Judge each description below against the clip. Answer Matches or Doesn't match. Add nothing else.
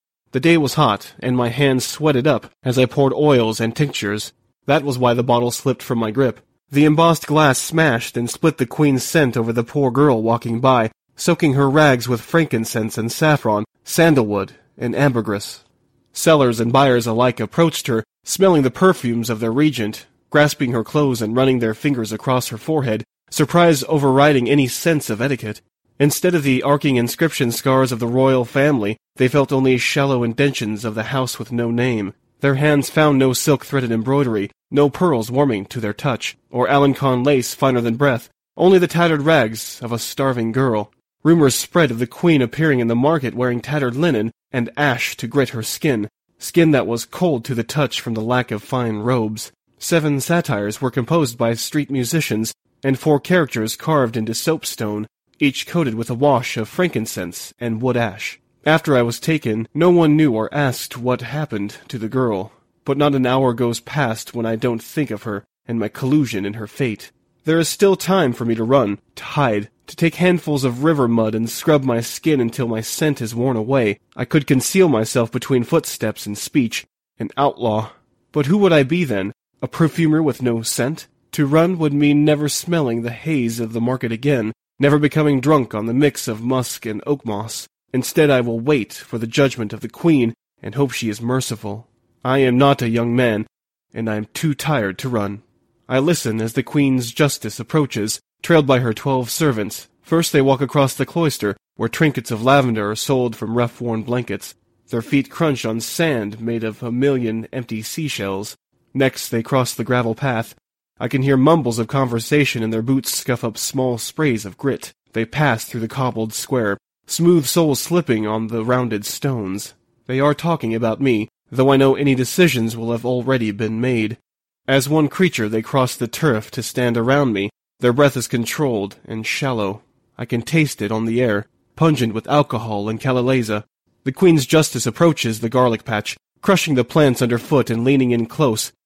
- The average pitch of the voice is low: Matches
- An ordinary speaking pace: Matches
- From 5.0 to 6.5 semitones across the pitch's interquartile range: Doesn't match